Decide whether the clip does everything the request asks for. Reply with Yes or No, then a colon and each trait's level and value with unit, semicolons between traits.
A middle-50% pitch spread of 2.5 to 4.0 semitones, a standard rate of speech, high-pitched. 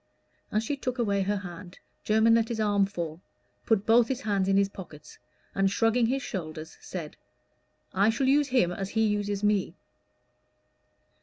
Yes: average, 2.9 semitones; average, 165 wpm; high, 205 Hz